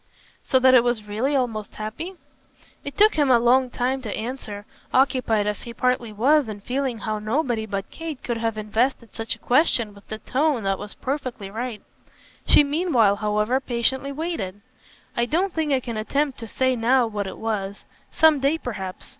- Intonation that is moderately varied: Yes, average, 4.0 semitones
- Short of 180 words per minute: No, average, 185 wpm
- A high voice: Yes, high, 240 Hz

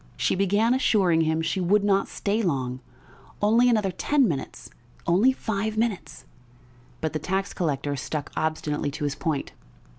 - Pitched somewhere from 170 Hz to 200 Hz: Yes, medium, 185 Hz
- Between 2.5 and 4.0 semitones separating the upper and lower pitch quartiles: No, average, 5.2 semitones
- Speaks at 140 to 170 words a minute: Yes, average, 150 wpm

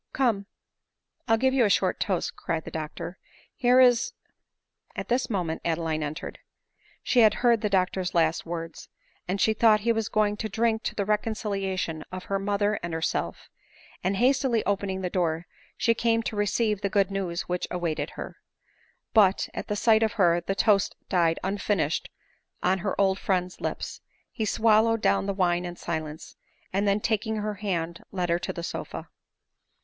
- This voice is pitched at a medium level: No, high, 195 Hz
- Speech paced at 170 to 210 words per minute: Yes, average, 175 wpm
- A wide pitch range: No, average, 3.7 semitones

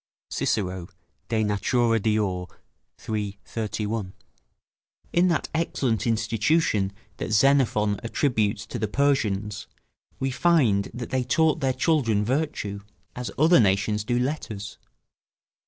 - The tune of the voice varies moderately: Yes, average, 4.4 semitones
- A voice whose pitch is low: Yes, low, 115 Hz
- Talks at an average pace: No, slow, 110 wpm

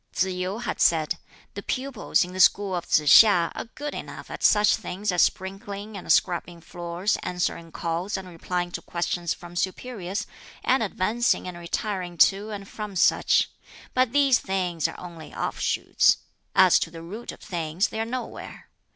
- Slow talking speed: No, average, 170 wpm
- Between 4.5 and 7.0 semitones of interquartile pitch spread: No, average, 3.4 semitones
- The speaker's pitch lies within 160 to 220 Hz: Yes, medium, 185 Hz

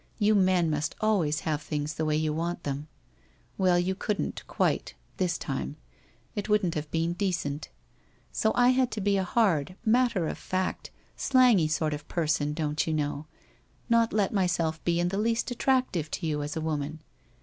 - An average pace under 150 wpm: No, average, 200 wpm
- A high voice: No, medium, 170 Hz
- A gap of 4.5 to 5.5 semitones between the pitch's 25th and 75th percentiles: Yes, average, 5.0 semitones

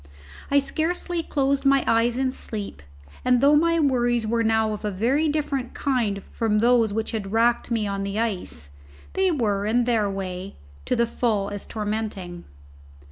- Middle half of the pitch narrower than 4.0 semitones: No, average, 4.4 semitones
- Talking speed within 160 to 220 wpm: Yes, average, 170 wpm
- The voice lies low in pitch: No, high, 230 Hz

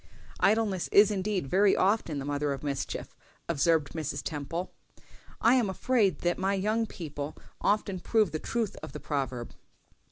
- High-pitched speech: No, medium, 180 Hz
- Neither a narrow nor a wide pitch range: No, wide, 6.0 semitones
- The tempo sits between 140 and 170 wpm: Yes, average, 155 wpm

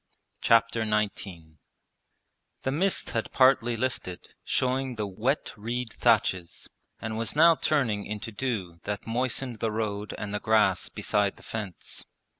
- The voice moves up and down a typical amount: Yes, average, 3.4 semitones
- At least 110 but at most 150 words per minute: Yes, slow, 135 wpm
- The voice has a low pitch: Yes, low, 110 Hz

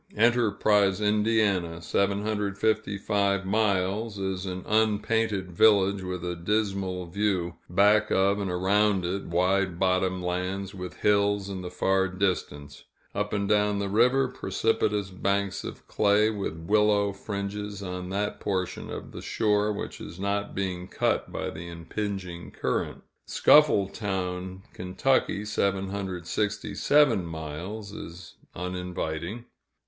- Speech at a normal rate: No, slow, 120 wpm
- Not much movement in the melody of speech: Yes, narrow, 2.2 semitones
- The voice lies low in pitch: Yes, low, 100 Hz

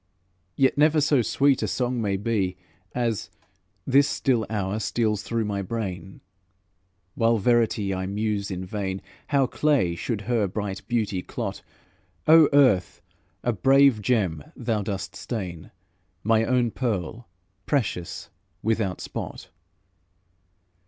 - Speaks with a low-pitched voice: Yes, low, 110 Hz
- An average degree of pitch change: Yes, average, 4.2 semitones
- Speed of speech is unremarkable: No, slow, 125 wpm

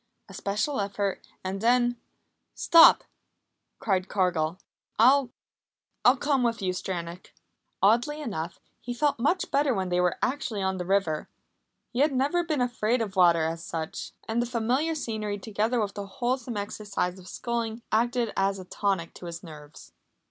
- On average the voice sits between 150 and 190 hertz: No, high, 215 Hz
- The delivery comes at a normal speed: Yes, average, 160 wpm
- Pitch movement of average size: Yes, average, 4.7 semitones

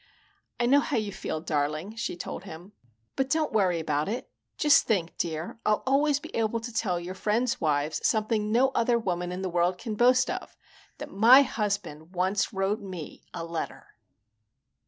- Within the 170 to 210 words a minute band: Yes, average, 180 wpm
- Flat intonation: No, average, 5.2 semitones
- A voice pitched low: No, high, 200 Hz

